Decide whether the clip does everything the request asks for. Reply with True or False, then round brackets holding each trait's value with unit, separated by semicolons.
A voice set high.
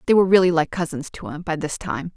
False (170 Hz)